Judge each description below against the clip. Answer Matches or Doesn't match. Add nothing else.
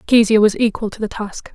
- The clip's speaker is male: Doesn't match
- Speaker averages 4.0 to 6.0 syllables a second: Matches